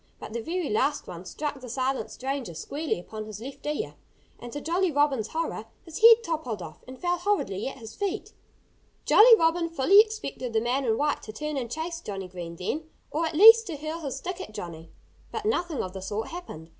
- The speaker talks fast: Yes, fast, 210 wpm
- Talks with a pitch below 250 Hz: No, very high, 280 Hz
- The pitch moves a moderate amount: No, wide, 7.4 semitones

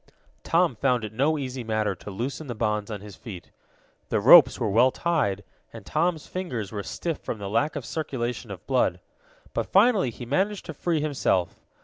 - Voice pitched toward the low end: Yes, low, 125 Hz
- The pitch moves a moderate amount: No, wide, 6.7 semitones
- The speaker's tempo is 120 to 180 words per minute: No, average, 190 wpm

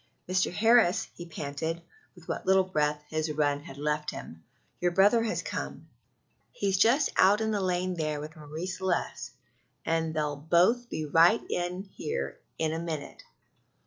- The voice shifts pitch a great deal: No, average, 3.8 semitones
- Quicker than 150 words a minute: Yes, average, 160 wpm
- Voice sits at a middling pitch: Yes, medium, 170 Hz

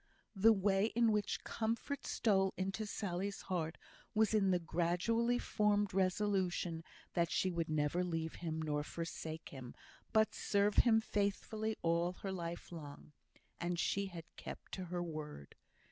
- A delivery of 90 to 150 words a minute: Yes, average, 145 wpm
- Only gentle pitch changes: No, average, 3.8 semitones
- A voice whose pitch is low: No, medium, 185 Hz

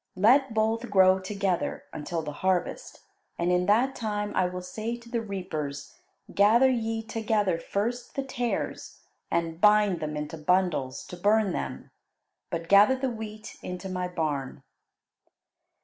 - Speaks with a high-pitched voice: Yes, high, 200 Hz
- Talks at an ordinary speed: Yes, average, 145 wpm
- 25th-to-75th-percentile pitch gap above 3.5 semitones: Yes, average, 4.0 semitones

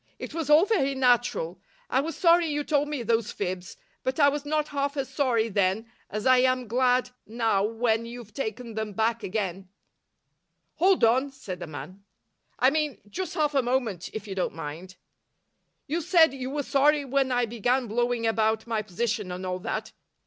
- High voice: Yes, high, 245 Hz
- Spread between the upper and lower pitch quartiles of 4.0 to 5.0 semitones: Yes, average, 4.7 semitones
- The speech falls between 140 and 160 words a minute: No, average, 185 wpm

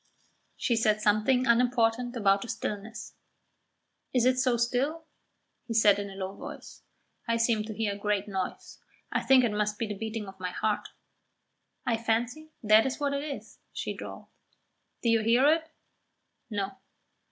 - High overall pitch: Yes, high, 225 Hz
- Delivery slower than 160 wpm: No, average, 165 wpm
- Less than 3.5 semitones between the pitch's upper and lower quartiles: Yes, average, 3.1 semitones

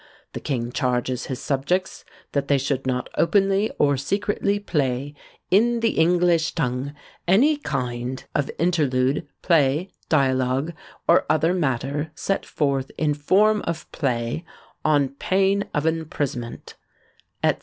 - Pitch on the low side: No, medium, 145 Hz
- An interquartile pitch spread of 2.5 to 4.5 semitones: No, average, 5.1 semitones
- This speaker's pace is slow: Yes, slow, 125 wpm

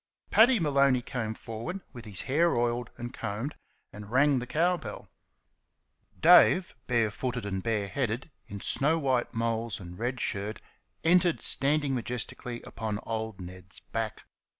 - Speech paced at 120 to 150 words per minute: Yes, average, 145 wpm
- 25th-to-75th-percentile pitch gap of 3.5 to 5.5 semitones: Yes, average, 4.4 semitones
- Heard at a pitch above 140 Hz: No, low, 120 Hz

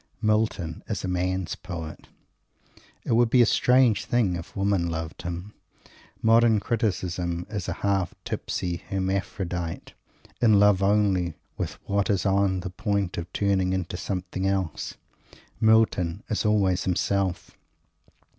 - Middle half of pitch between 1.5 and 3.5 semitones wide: Yes, average, 2.7 semitones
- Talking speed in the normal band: No, slow, 130 wpm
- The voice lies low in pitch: Yes, very low, 95 Hz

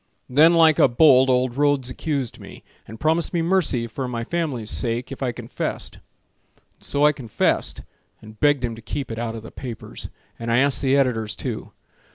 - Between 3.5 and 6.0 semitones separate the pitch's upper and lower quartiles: Yes, average, 3.8 semitones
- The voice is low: Yes, low, 130 Hz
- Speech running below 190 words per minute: No, average, 195 wpm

